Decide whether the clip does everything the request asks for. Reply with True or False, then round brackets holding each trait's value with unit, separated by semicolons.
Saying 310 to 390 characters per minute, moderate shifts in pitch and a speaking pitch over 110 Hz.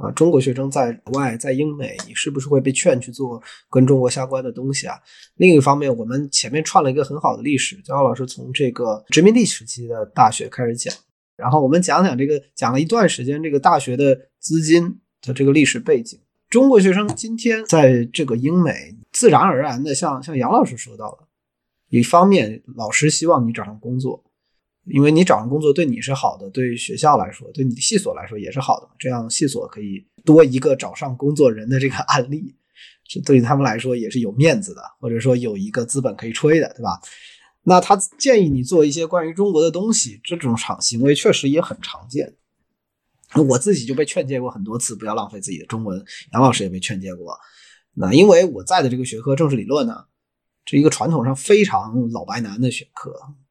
True (320 characters per minute; 4.8 semitones; 135 Hz)